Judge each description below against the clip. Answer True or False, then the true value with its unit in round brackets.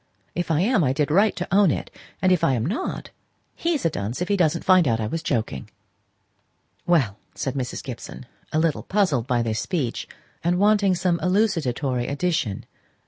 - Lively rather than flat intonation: True (6.6 semitones)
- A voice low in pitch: False (165 Hz)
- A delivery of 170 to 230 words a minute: True (180 wpm)